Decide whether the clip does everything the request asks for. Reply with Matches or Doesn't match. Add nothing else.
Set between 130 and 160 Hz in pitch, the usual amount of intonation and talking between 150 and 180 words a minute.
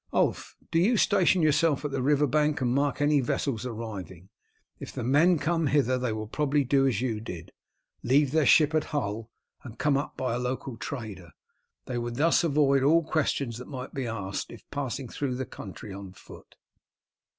Doesn't match